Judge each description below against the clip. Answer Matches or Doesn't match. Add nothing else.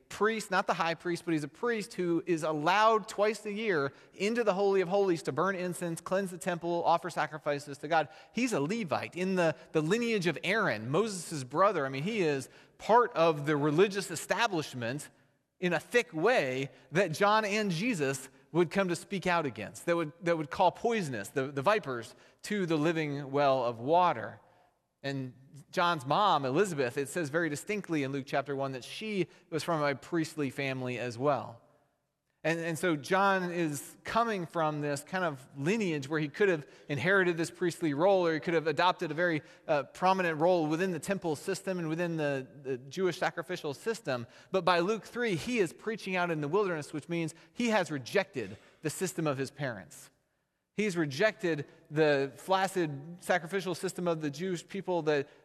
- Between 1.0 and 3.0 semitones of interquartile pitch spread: Doesn't match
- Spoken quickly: Doesn't match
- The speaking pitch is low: Doesn't match